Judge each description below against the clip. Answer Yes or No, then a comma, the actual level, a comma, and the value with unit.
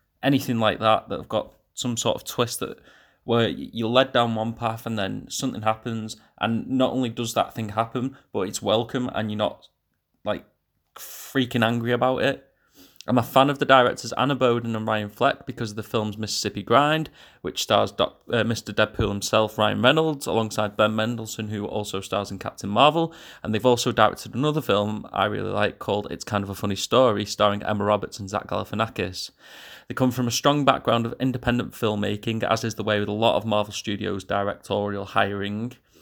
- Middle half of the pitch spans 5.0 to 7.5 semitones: No, average, 2.8 semitones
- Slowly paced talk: No, average, 195 wpm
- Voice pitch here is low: Yes, low, 110 Hz